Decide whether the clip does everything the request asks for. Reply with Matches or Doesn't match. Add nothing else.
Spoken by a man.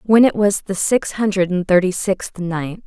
Doesn't match